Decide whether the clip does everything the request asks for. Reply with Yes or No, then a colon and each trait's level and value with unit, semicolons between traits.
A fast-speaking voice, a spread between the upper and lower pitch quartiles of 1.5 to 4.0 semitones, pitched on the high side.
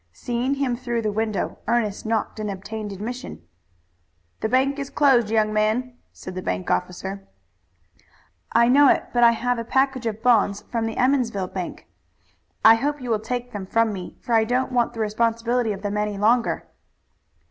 No: average, 180 wpm; average, 2.9 semitones; high, 230 Hz